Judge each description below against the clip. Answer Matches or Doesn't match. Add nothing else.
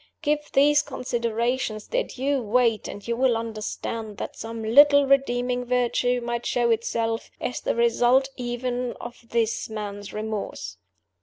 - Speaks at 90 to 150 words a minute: Matches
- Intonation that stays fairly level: Matches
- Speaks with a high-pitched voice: Matches